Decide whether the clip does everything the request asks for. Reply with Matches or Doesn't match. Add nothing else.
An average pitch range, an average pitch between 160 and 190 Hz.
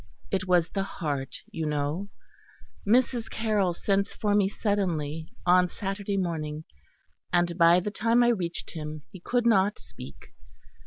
Matches